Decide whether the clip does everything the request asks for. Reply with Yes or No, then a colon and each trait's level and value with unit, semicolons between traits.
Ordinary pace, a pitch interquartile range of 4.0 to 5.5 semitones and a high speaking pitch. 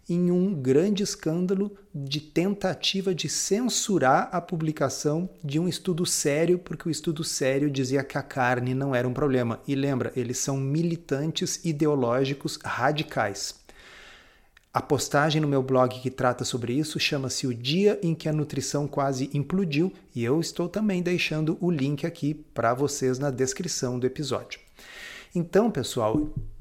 No: average, 150 wpm; average, 4.5 semitones; medium, 150 Hz